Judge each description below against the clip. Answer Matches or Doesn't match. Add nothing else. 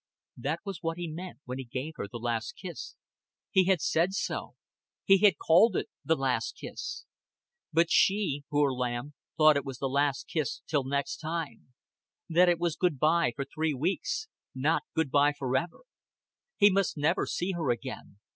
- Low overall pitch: Doesn't match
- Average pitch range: Matches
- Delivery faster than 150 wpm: Matches